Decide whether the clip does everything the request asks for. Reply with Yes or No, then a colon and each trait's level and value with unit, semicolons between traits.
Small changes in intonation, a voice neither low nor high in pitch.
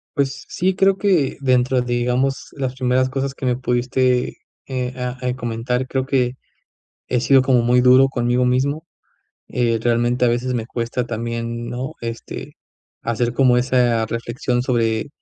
No: narrow, 1.6 semitones; low, 125 Hz